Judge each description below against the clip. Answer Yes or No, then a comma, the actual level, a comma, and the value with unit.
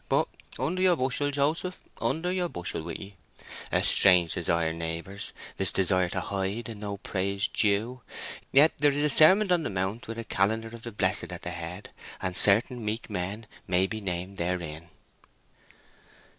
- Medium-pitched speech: No, low, 100 Hz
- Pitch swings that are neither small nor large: No, wide, 5.8 semitones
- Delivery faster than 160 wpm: Yes, average, 170 wpm